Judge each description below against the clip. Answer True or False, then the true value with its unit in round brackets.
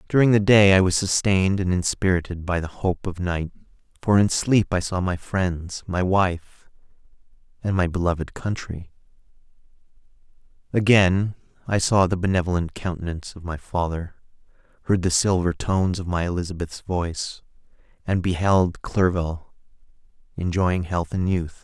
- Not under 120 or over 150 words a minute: True (140 wpm)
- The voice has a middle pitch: False (90 Hz)